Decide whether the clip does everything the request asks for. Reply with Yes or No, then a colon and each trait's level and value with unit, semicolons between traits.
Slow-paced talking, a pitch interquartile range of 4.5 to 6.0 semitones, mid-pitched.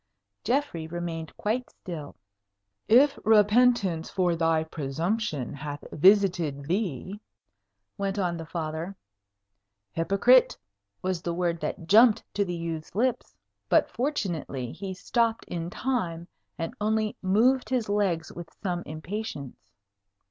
Yes: slow, 120 wpm; average, 4.8 semitones; medium, 180 Hz